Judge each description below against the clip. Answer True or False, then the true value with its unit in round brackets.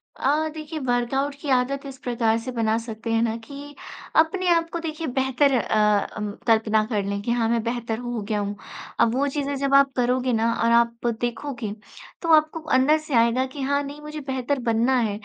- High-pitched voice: True (250 Hz)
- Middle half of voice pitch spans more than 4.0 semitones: False (3.7 semitones)